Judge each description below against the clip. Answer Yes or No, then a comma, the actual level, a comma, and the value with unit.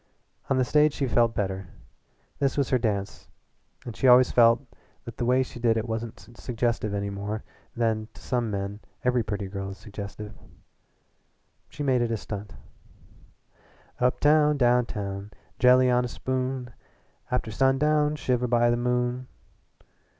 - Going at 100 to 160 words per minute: Yes, average, 150 wpm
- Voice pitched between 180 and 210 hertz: No, low, 120 Hz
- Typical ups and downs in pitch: Yes, average, 3.2 semitones